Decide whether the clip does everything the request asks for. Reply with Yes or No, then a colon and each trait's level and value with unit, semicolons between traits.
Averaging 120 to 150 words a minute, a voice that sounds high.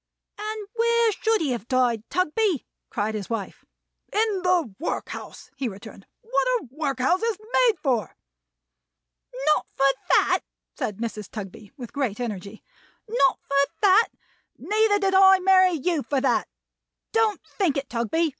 Yes: average, 140 wpm; very high, 310 Hz